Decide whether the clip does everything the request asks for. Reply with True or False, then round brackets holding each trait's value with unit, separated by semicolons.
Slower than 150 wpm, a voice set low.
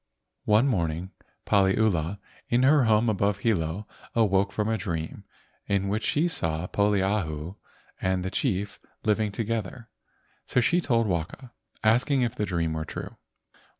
True (140 wpm; 105 Hz)